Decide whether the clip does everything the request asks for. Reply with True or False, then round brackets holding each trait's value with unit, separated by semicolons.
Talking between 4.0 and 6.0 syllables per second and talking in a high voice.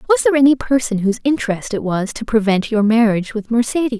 False (6.6 syllables/s; 225 Hz)